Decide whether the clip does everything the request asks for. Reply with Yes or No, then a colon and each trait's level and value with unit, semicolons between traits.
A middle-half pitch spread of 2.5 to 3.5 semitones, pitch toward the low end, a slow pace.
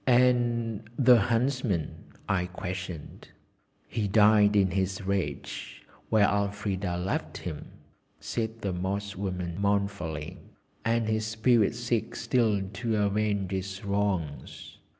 Yes: average, 2.9 semitones; low, 100 Hz; slow, 110 wpm